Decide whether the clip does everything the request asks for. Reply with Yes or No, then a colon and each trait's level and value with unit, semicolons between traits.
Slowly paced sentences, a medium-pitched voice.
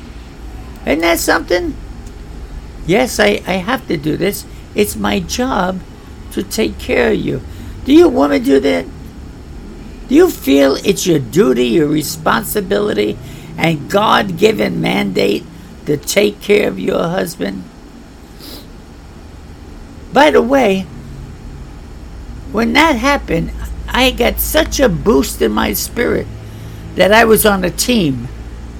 Yes: slow, 130 wpm; medium, 150 Hz